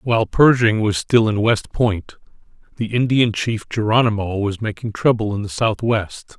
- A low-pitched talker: Yes, low, 110 Hz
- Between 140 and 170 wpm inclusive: Yes, average, 160 wpm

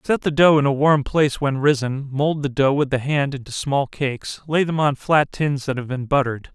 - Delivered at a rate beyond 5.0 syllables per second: Yes, 5.2 syllables/s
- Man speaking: Yes, male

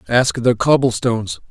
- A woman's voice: No, male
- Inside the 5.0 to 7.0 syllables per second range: No, 4.7 syllables/s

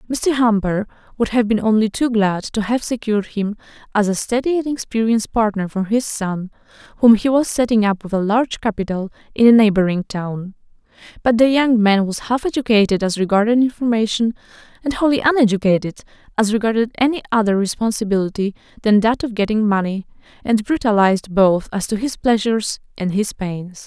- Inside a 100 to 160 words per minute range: No, average, 170 wpm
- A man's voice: No, female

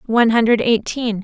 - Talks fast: No, average, 145 wpm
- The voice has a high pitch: Yes, high, 225 Hz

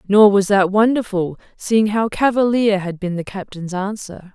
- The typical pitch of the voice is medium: No, high, 200 Hz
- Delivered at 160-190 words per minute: Yes, average, 165 wpm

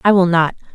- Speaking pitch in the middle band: Yes, medium, 180 Hz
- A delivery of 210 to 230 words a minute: No, fast, 245 wpm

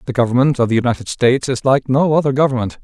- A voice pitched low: Yes, low, 125 Hz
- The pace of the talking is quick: Yes, fast, 235 wpm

